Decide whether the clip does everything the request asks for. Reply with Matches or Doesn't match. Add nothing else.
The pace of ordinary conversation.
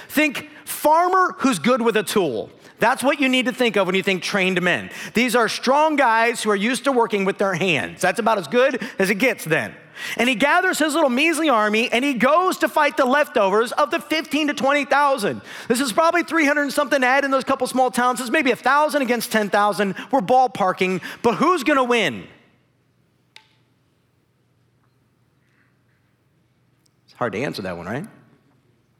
Matches